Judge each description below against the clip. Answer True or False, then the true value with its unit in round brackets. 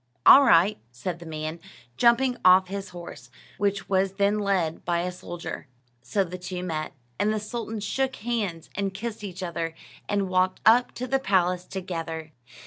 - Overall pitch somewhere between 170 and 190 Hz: True (185 Hz)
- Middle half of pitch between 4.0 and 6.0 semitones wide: False (3.3 semitones)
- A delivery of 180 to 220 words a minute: False (170 wpm)